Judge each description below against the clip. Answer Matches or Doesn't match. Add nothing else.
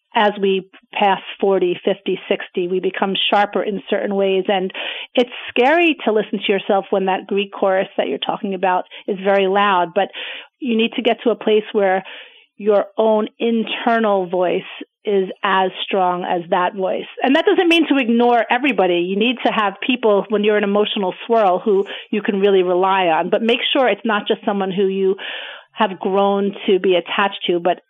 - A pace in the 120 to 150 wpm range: Doesn't match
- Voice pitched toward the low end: Doesn't match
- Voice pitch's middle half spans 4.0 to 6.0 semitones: Doesn't match